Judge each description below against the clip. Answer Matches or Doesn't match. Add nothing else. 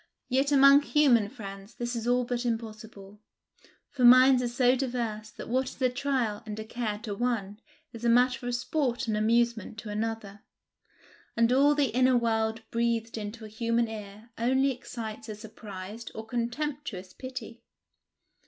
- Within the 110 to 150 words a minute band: Doesn't match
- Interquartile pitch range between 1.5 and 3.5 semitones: Matches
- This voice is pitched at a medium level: Doesn't match